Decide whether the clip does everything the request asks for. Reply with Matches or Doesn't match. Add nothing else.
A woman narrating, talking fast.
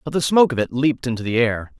Doesn't match